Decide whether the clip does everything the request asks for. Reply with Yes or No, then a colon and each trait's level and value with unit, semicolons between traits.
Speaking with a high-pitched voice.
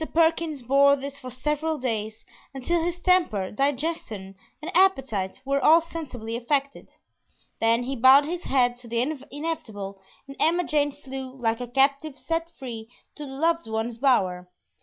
Yes: very high, 270 Hz